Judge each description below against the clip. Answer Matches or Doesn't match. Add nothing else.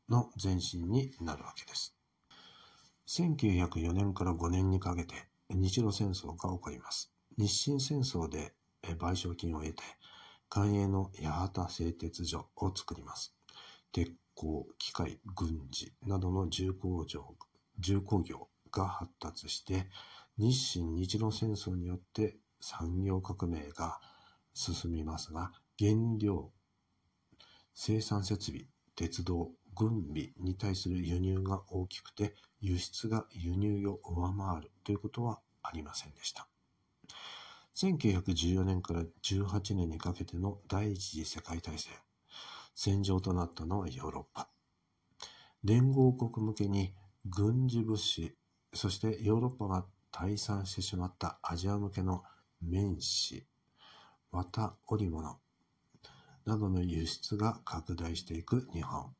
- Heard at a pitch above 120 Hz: Doesn't match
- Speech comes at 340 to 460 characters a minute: Doesn't match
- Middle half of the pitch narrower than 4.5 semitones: Matches